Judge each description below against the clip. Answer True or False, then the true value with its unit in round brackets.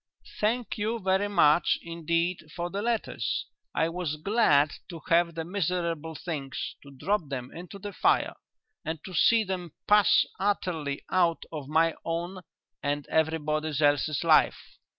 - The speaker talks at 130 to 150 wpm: True (145 wpm)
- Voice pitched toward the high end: False (170 Hz)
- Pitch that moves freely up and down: False (3.7 semitones)